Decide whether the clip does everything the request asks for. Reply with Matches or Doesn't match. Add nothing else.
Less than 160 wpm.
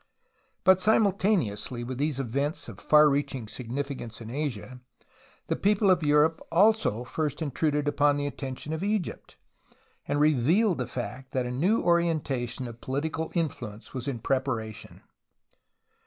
Matches